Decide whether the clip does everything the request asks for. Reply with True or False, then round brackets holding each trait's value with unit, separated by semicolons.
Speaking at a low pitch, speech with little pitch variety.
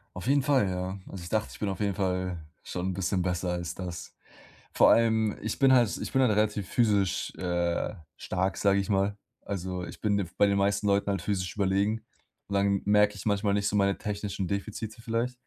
True (100 Hz; 2.1 semitones)